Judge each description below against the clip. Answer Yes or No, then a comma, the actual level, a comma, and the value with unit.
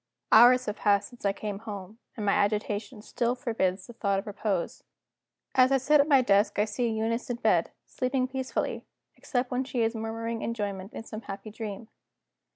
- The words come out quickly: No, average, 185 wpm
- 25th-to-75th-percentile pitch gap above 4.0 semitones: No, average, 3.2 semitones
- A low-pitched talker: No, high, 225 Hz